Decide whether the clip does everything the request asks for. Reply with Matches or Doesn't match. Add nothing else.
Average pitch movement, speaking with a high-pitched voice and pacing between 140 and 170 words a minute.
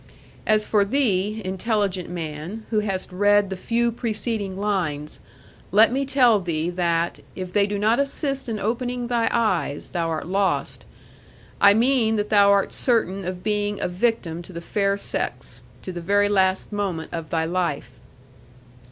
Matches